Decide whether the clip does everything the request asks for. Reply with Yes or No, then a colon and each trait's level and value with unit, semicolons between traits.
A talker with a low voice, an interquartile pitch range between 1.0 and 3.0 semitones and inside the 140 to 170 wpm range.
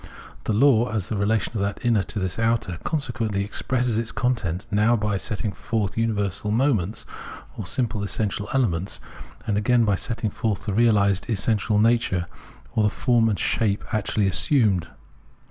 Yes: low, 110 Hz; narrow, 2.6 semitones; average, 160 wpm